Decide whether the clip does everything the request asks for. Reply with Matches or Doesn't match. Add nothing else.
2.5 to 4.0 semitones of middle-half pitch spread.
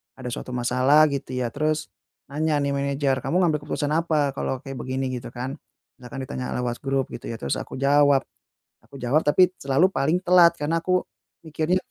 Matches